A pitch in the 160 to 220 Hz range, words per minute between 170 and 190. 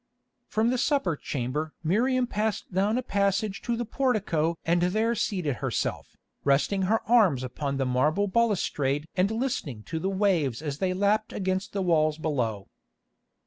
No: medium, 185 Hz; average, 155 wpm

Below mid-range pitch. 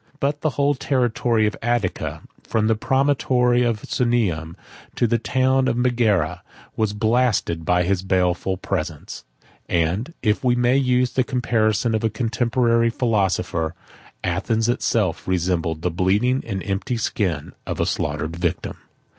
Yes: low, 110 Hz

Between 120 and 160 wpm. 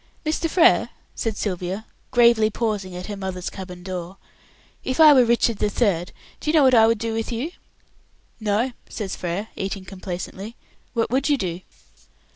No: average, 170 wpm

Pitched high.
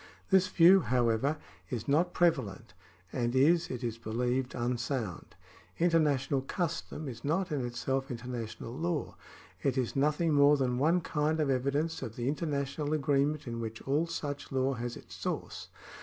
No: medium, 140 Hz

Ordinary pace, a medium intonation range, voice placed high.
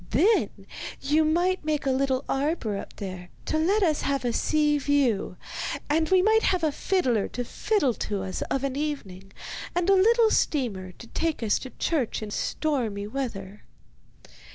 No: average, 170 wpm; wide, 6.7 semitones; very high, 280 Hz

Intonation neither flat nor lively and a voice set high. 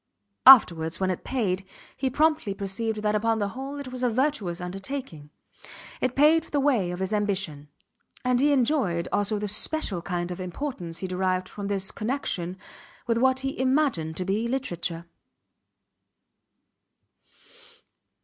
No: wide, 6.3 semitones; high, 210 Hz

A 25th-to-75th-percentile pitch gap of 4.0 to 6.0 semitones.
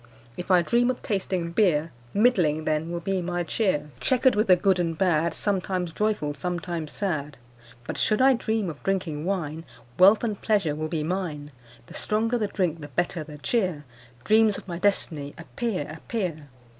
Yes: average, 4.7 semitones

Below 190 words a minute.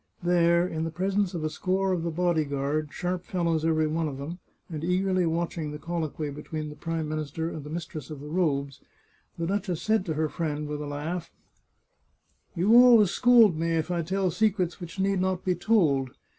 No: fast, 205 wpm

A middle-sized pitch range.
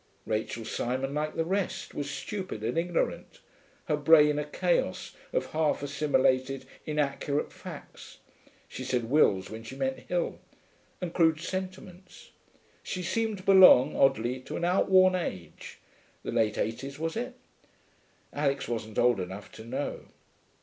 No: wide, 6.0 semitones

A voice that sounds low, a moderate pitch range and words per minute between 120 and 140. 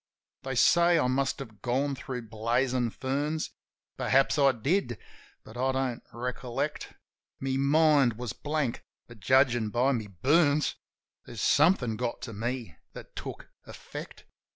Yes: low, 130 Hz; average, 3.1 semitones; slow, 135 wpm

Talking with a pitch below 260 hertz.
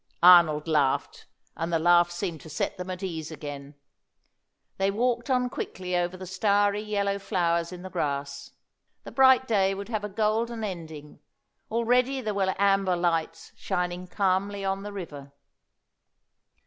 Yes: medium, 185 Hz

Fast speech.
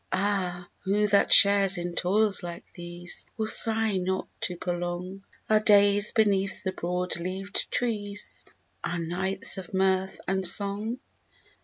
No: slow, 135 wpm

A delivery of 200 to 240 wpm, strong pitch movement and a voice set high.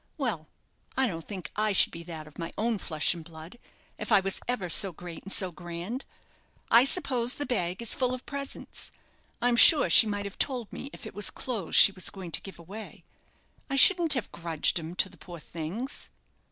Yes: fast, 205 wpm; wide, 6.3 semitones; high, 200 Hz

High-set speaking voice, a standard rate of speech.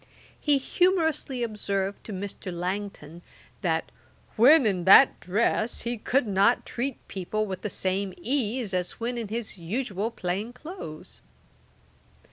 No: high, 210 Hz; slow, 130 wpm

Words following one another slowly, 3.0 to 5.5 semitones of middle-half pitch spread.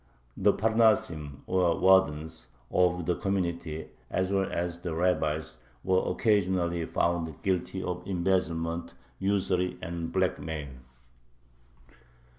No: slow, 100 wpm; narrow, 2.4 semitones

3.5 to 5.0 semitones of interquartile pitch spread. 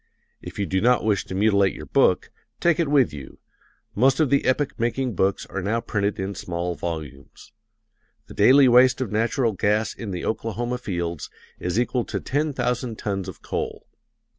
Yes: average, 4.6 semitones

